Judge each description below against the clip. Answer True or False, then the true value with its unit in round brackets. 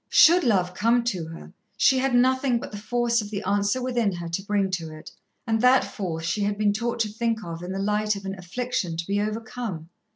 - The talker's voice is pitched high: True (210 Hz)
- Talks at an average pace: False (230 wpm)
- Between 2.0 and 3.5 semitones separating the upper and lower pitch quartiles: False (4.1 semitones)